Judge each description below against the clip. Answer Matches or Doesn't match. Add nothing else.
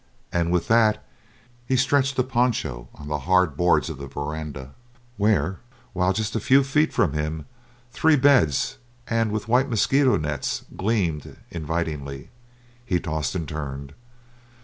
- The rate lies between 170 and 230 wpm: Doesn't match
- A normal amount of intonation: Doesn't match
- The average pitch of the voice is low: Matches